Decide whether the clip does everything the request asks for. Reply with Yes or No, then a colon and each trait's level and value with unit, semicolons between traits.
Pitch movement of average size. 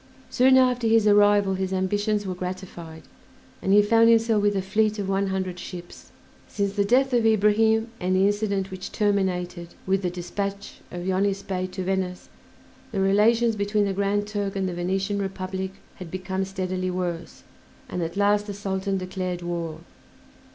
No: narrow, 1.9 semitones